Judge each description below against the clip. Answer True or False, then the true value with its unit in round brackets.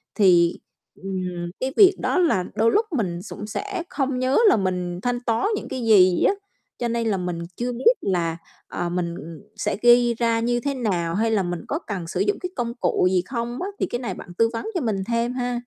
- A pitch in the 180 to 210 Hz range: False (230 Hz)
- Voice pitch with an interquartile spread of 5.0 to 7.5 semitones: True (5.3 semitones)